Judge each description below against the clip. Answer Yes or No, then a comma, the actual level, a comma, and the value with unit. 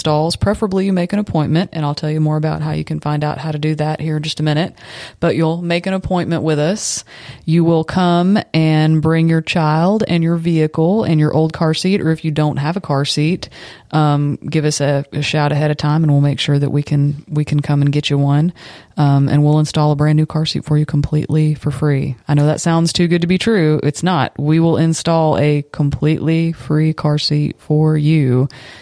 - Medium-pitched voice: Yes, medium, 155 Hz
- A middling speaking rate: No, fast, 235 wpm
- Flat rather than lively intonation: Yes, narrow, 1.7 semitones